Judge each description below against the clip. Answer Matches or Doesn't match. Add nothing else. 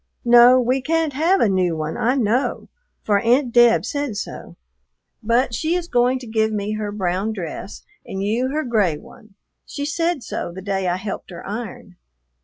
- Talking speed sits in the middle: Matches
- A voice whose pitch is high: Matches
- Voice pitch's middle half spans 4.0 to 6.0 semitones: Matches